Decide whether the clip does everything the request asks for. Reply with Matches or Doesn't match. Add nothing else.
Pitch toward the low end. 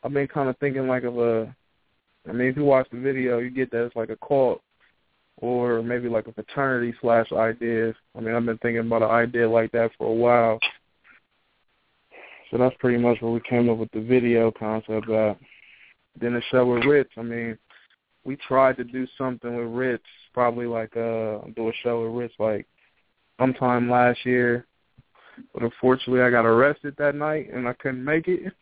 Matches